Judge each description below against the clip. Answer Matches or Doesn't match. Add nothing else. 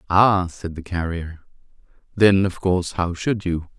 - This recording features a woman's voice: Doesn't match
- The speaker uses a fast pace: Doesn't match